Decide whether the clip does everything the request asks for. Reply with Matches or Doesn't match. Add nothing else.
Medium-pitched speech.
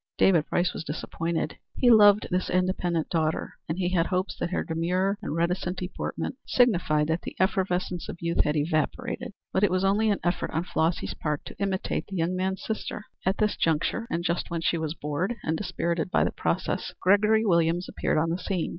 Matches